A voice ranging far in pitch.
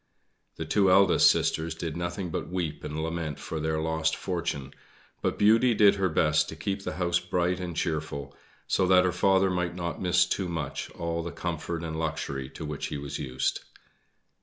No: narrow, 2.6 semitones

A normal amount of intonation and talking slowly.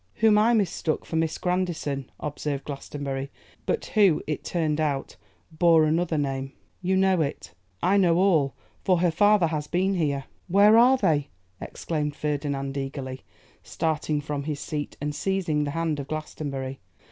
No: average, 3.9 semitones; average, 155 wpm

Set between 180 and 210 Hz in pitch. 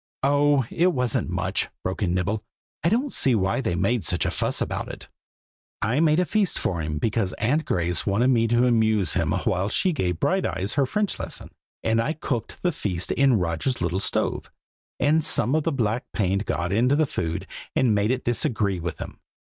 No: low, 115 Hz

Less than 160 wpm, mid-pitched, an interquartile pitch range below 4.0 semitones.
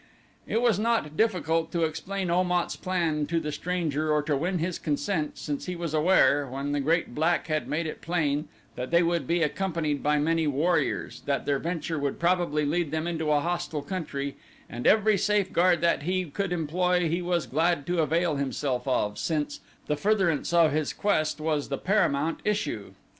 No: average, 185 wpm; medium, 165 Hz; average, 3.2 semitones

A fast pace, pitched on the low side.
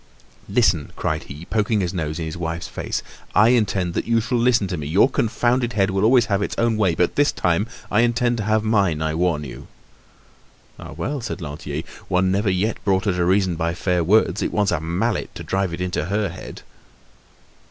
Yes: fast, 210 wpm; very low, 95 Hz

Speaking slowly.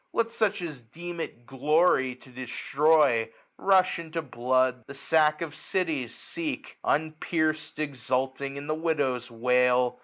Yes: slow, 130 wpm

